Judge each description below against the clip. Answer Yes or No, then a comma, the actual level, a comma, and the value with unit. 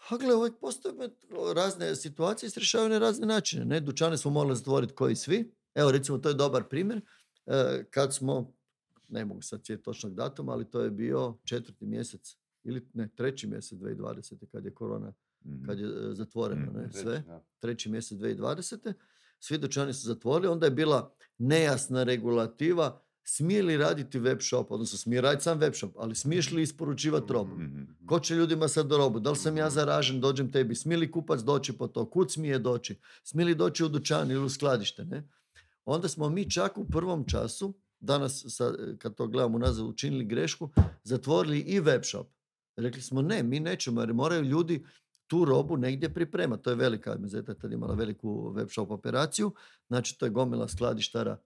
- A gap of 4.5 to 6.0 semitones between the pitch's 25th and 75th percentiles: Yes, average, 5.3 semitones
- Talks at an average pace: No, fast, 180 wpm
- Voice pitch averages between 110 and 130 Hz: No, medium, 140 Hz